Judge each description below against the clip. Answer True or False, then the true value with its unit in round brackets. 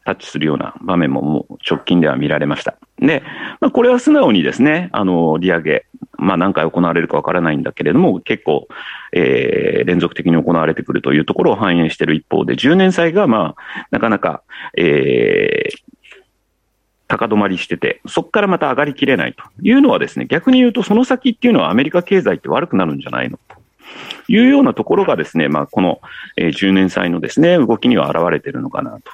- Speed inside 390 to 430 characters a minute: True (405 characters per minute)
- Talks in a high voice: True (195 Hz)